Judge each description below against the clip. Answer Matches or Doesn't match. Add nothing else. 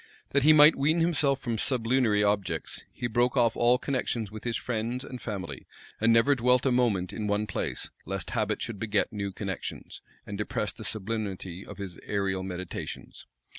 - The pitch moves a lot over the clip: Doesn't match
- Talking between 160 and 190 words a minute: Matches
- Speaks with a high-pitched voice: Doesn't match